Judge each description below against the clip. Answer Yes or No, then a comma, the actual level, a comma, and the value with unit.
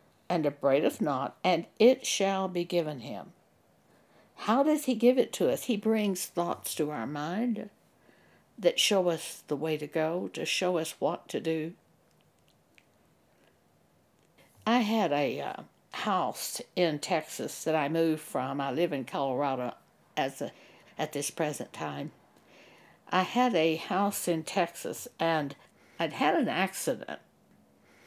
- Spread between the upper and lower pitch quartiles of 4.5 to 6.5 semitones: Yes, average, 5.2 semitones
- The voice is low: No, medium, 175 Hz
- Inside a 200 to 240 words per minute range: No, average, 140 wpm